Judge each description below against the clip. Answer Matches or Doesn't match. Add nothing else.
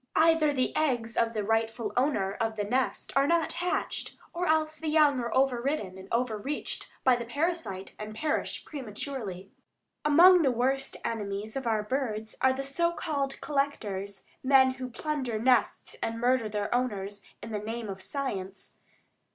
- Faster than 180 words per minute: Doesn't match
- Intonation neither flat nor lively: Matches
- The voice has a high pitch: Matches